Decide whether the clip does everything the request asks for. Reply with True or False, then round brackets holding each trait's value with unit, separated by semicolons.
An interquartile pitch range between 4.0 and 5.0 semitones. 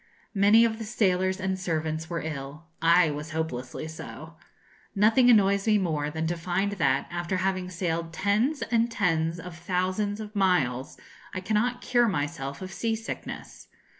True (4.3 semitones)